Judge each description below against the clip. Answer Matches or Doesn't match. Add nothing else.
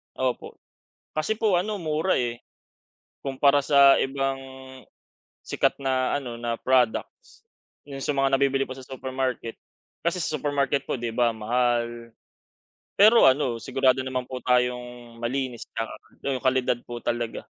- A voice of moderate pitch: Doesn't match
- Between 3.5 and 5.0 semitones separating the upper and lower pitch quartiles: Doesn't match